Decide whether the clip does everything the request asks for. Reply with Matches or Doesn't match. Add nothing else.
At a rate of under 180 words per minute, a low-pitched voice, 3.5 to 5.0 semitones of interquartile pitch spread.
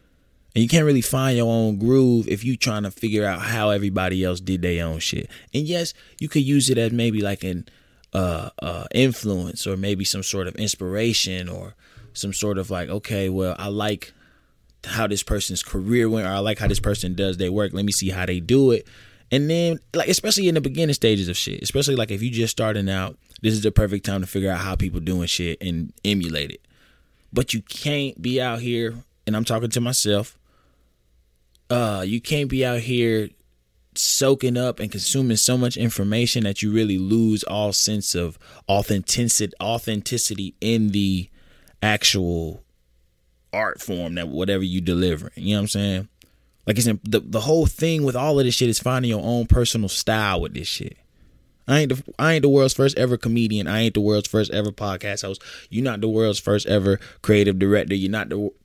Doesn't match